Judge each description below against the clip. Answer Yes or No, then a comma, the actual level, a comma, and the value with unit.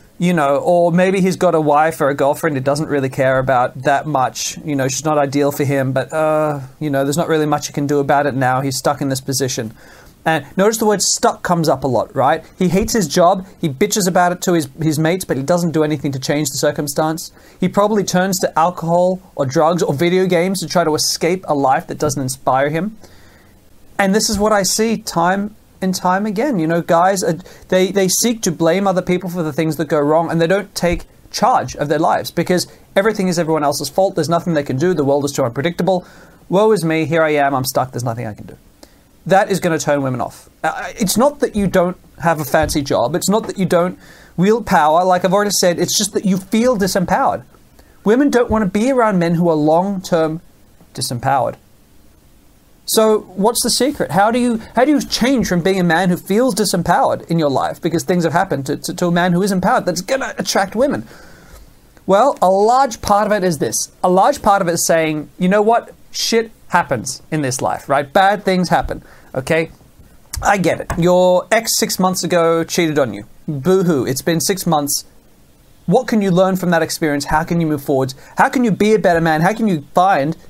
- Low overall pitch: No, medium, 175 Hz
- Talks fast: Yes, fast, 230 wpm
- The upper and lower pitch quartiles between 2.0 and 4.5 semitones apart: Yes, average, 4.2 semitones